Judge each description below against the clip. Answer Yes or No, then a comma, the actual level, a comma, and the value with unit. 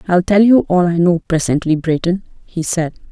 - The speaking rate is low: No, average, 195 wpm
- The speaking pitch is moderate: Yes, medium, 175 Hz